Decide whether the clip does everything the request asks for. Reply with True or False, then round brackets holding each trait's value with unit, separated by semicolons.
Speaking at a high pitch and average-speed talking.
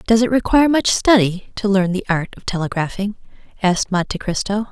True (205 Hz; 180 wpm)